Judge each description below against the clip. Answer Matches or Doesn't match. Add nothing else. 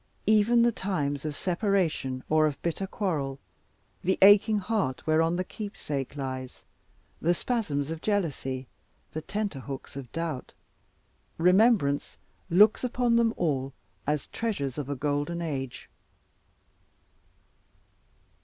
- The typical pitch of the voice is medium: Matches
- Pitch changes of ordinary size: Doesn't match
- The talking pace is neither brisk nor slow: Doesn't match